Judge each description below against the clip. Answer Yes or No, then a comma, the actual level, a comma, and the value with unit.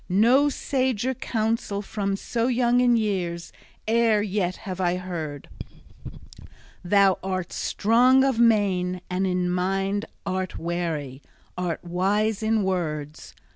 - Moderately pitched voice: No, high, 195 Hz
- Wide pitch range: No, average, 3.8 semitones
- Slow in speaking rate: Yes, slow, 120 wpm